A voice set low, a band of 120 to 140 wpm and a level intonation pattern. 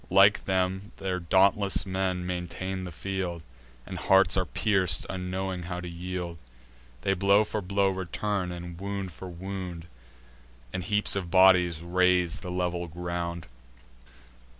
Yes: very low, 90 Hz; slow, 135 wpm; narrow, 1.6 semitones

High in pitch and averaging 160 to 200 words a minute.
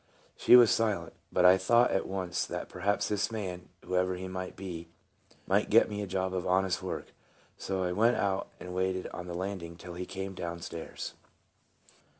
No: very low, 95 Hz; average, 190 wpm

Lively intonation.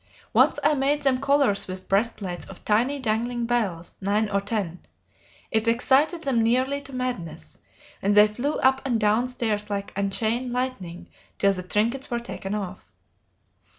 No: average, 4.3 semitones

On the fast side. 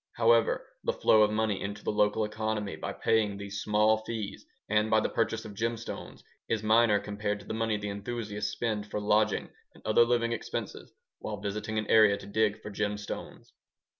No: average, 185 wpm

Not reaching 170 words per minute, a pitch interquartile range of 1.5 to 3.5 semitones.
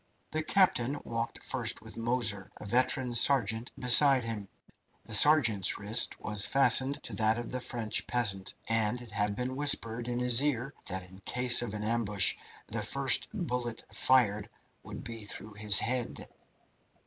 Yes: average, 160 wpm; average, 3.0 semitones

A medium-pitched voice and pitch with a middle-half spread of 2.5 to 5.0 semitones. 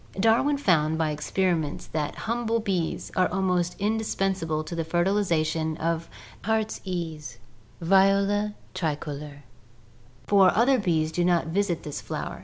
Yes: medium, 175 Hz; average, 4.1 semitones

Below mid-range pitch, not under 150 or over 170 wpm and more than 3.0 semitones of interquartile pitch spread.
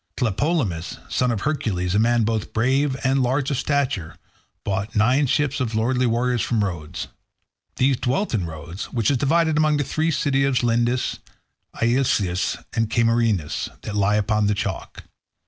Yes: low, 120 Hz; average, 160 wpm; average, 4.6 semitones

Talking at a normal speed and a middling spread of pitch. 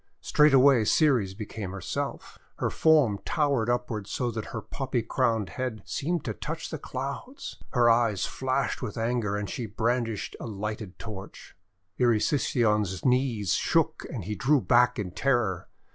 Yes: average, 145 wpm; average, 3.9 semitones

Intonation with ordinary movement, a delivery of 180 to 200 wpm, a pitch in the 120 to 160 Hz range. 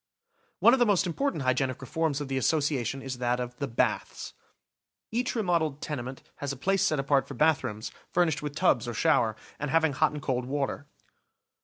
Yes: average, 3.7 semitones; average, 190 wpm; medium, 140 Hz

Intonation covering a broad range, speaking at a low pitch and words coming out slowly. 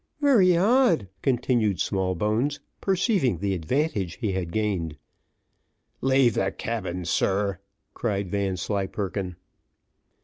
Yes: wide, 6.0 semitones; low, 105 Hz; slow, 95 wpm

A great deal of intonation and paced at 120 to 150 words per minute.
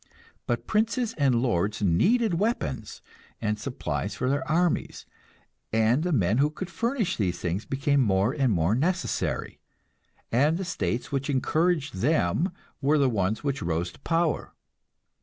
Yes: wide, 7.8 semitones; average, 145 wpm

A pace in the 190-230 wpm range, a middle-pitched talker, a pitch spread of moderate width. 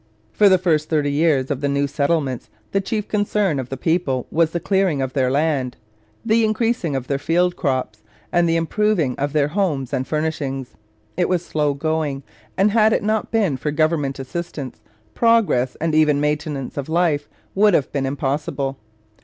No: average, 180 wpm; medium, 155 Hz; average, 4.4 semitones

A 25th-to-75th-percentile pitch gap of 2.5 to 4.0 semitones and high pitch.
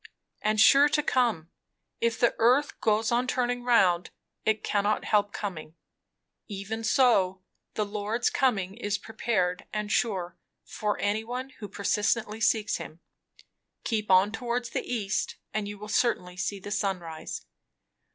Yes: average, 3.0 semitones; high, 215 Hz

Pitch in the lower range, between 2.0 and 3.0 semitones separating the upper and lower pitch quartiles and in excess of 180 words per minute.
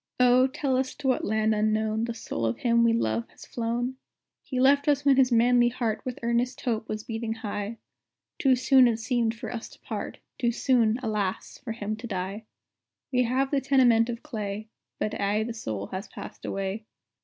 No: high, 230 Hz; narrow, 2.6 semitones; average, 195 wpm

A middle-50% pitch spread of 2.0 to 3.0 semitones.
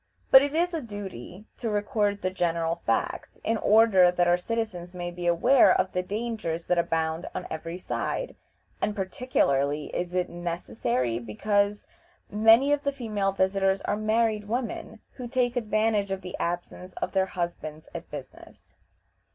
No: average, 4.3 semitones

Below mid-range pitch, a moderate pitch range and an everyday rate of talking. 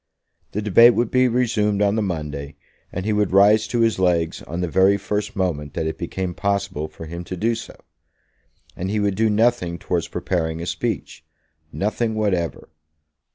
Yes: low, 100 Hz; average, 3.9 semitones; average, 180 wpm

